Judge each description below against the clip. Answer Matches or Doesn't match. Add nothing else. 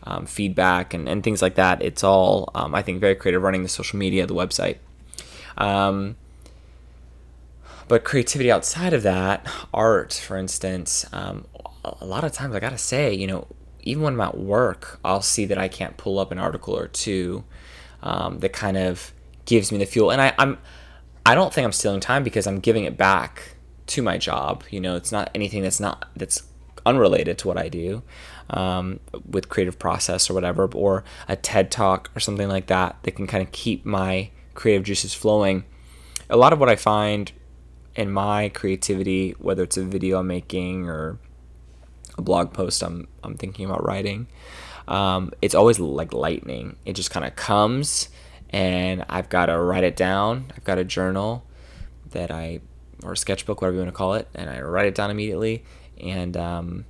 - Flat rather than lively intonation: Doesn't match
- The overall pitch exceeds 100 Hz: Doesn't match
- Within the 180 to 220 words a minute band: Matches